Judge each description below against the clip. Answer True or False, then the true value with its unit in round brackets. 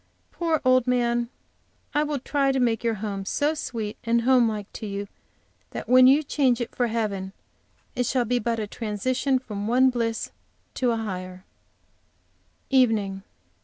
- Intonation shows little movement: False (3.3 semitones)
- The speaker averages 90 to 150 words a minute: False (165 wpm)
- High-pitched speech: True (235 Hz)